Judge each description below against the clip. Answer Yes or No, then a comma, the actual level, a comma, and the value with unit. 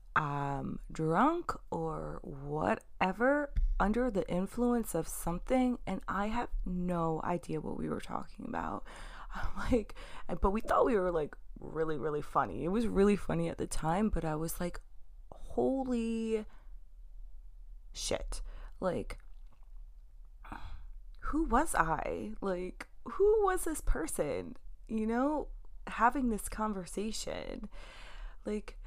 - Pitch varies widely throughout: Yes, wide, 6.7 semitones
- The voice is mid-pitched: No, high, 200 Hz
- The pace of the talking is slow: Yes, slow, 120 wpm